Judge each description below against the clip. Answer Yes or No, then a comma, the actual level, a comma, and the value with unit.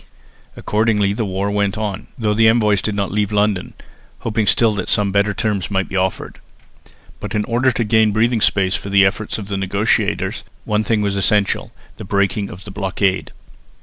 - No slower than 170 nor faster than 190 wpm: Yes, average, 185 wpm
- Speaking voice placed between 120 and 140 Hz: No, low, 105 Hz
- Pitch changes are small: Yes, narrow, 1.6 semitones